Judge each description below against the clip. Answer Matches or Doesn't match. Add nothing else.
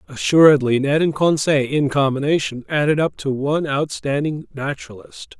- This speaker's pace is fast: Doesn't match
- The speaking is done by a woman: Doesn't match